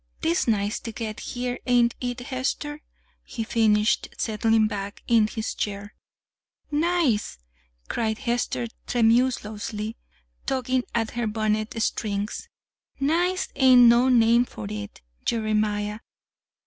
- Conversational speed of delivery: No, slow, 110 wpm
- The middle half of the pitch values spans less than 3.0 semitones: Yes, narrow, 2.6 semitones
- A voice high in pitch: Yes, high, 230 Hz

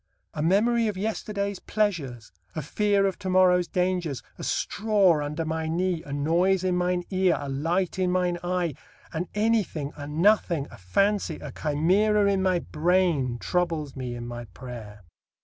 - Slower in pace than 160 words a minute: No, average, 165 wpm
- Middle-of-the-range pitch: Yes, medium, 180 Hz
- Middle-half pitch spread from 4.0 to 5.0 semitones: Yes, average, 4.4 semitones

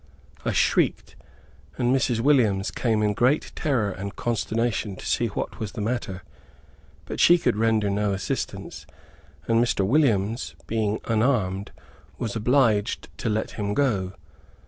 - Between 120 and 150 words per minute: Yes, average, 140 wpm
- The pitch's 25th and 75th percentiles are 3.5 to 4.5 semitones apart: No, average, 3.1 semitones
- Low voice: Yes, low, 110 Hz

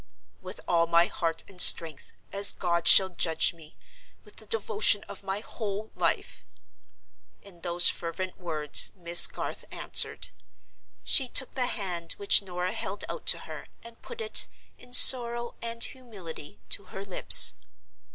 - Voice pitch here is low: No, high, 190 Hz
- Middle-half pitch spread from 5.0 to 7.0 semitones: Yes, average, 5.3 semitones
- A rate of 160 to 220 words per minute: No, average, 145 wpm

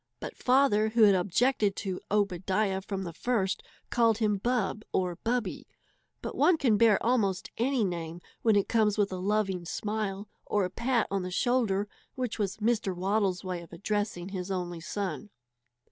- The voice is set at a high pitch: Yes, high, 205 Hz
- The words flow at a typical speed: Yes, average, 170 wpm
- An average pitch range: Yes, average, 3.1 semitones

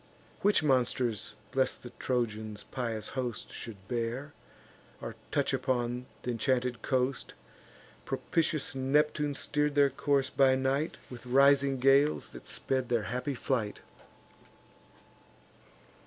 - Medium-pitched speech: No, low, 130 Hz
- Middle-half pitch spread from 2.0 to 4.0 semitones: Yes, narrow, 2.5 semitones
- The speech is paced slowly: Yes, slow, 110 wpm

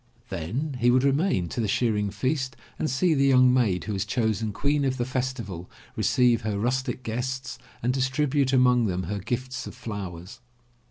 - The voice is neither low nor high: No, low, 125 Hz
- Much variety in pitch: No, average, 3.7 semitones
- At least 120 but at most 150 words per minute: No, average, 180 wpm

